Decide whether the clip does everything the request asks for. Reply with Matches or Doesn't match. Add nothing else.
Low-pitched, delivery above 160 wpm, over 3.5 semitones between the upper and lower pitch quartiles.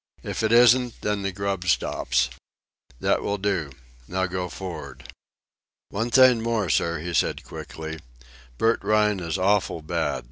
Doesn't match